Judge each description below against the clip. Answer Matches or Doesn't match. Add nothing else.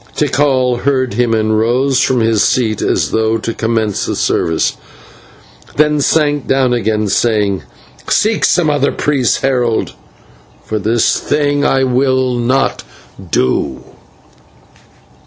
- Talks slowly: Matches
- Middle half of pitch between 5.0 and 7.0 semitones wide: Doesn't match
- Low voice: Matches